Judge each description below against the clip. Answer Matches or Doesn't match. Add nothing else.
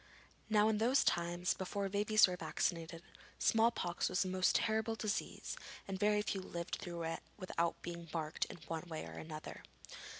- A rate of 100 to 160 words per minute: Doesn't match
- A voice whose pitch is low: Doesn't match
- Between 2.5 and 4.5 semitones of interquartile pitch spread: Matches